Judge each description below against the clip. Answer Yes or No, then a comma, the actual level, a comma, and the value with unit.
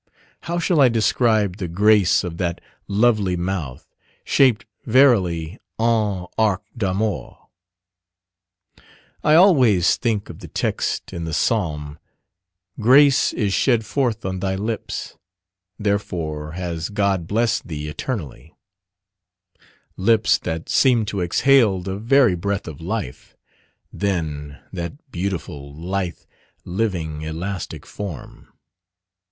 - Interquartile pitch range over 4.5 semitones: Yes, average, 4.9 semitones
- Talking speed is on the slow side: Yes, slow, 110 wpm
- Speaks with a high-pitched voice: No, low, 100 Hz